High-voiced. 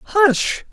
Yes: very high, 350 Hz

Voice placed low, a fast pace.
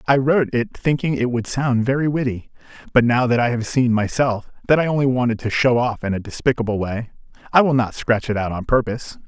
Yes: low, 120 Hz; fast, 225 wpm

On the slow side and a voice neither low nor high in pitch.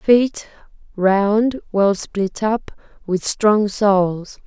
No: slow, 95 wpm; high, 205 Hz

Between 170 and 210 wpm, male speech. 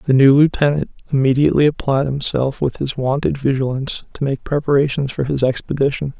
No: average, 155 wpm; male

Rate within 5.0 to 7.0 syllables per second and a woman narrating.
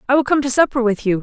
No: 7.6 syllables/s; female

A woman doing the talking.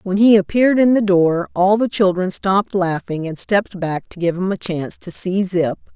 Yes: female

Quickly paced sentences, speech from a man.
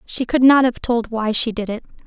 No: fast, 260 wpm; female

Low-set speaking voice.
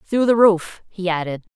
No: high, 190 Hz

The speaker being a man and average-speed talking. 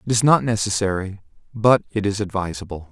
Yes: male; average, 165 wpm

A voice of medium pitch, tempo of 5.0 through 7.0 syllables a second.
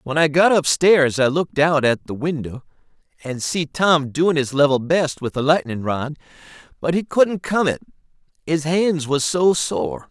No: medium, 150 Hz; 4.5 syllables/s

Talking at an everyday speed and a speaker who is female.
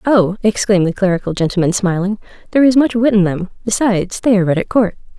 No: fast, 210 wpm; female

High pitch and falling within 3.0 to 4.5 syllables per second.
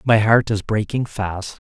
No: low, 105 Hz; 4.0 syllables/s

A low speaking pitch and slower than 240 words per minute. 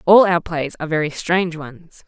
No: medium, 165 Hz; average, 200 wpm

